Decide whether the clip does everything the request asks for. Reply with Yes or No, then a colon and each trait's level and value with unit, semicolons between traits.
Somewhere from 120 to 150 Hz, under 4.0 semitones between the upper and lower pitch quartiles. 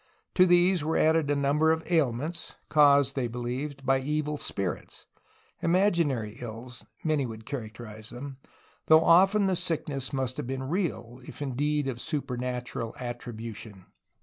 No: low, 135 Hz; average, 4.4 semitones